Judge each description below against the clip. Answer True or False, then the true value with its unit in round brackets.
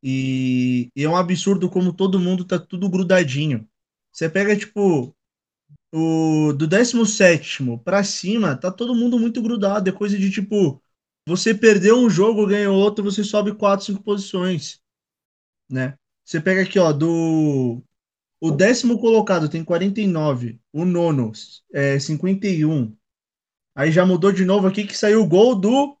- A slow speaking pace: False (150 wpm)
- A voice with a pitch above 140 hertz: True (185 Hz)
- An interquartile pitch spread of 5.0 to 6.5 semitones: True (5.4 semitones)